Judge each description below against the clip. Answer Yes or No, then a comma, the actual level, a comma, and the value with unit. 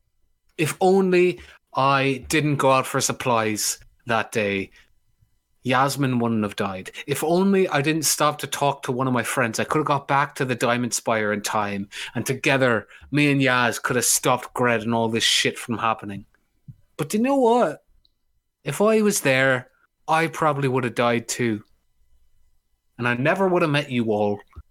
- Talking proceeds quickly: No, average, 180 wpm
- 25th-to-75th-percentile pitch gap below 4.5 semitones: No, average, 4.8 semitones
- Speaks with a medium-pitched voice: No, low, 130 Hz